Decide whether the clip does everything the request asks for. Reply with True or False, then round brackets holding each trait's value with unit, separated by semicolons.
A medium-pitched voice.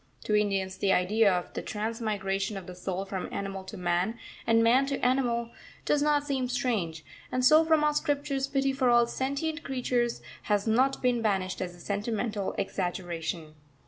False (225 Hz)